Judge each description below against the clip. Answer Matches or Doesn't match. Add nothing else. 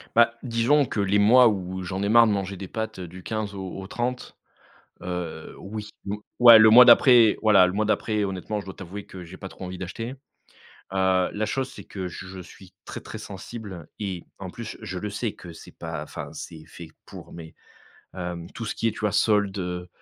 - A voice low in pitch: Matches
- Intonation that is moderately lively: Matches